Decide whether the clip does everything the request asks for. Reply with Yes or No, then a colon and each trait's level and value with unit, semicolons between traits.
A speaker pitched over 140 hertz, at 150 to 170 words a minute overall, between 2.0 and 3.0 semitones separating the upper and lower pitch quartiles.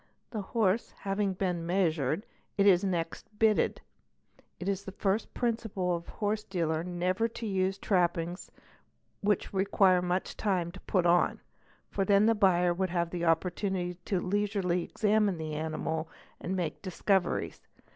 Yes: medium, 185 Hz; average, 155 wpm; narrow, 2.6 semitones